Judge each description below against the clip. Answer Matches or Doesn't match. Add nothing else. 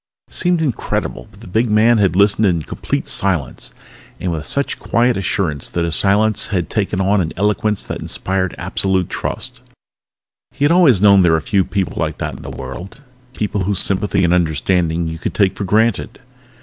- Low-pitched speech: Matches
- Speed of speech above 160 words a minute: Matches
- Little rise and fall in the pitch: Doesn't match